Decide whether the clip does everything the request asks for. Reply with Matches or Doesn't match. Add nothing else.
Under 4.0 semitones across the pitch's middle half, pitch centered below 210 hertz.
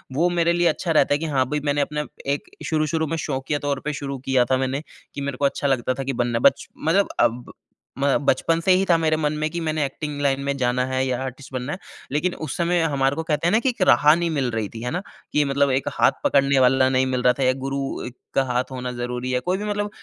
Matches